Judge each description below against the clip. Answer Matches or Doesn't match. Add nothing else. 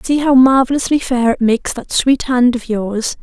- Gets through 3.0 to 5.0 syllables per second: Matches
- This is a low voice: Doesn't match